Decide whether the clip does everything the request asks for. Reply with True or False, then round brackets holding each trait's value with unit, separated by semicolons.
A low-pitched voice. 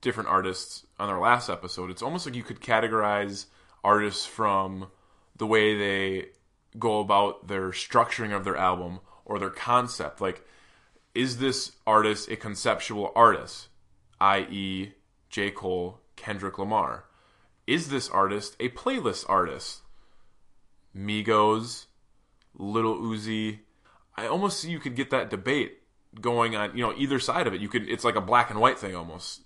True (105 Hz)